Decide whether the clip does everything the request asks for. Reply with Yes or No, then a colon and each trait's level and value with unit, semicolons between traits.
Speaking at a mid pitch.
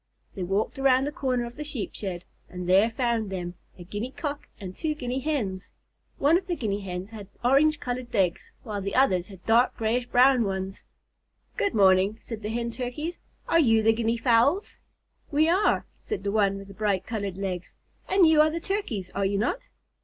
No: high, 225 Hz